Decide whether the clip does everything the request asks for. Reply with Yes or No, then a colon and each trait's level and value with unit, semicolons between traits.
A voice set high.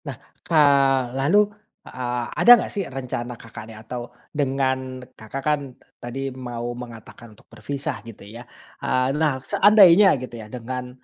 No: low, 130 Hz